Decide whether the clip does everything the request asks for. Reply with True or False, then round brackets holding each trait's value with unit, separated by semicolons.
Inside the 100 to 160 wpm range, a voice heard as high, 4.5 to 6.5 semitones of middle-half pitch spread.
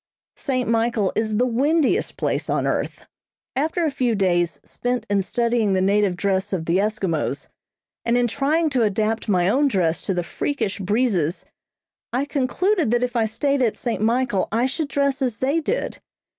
False (175 wpm; 235 Hz; 5.4 semitones)